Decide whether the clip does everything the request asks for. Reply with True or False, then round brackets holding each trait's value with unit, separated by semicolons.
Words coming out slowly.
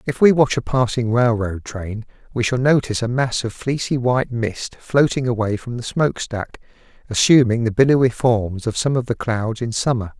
False (190 wpm)